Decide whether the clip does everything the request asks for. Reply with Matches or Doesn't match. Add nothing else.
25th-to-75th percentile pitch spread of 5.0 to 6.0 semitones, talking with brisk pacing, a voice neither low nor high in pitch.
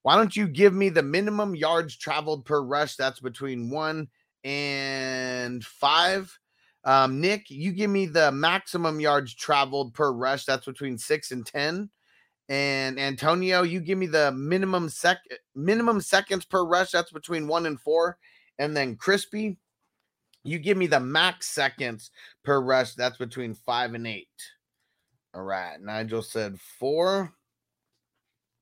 Doesn't match